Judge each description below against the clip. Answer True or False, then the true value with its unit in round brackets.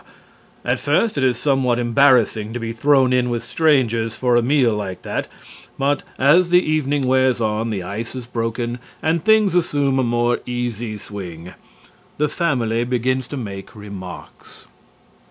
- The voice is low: True (120 Hz)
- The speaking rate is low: False (155 wpm)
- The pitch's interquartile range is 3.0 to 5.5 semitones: True (3.5 semitones)